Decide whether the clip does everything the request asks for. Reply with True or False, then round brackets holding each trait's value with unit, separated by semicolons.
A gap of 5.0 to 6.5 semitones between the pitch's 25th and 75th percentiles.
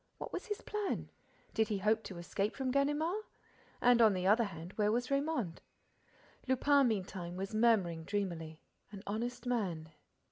True (5.3 semitones)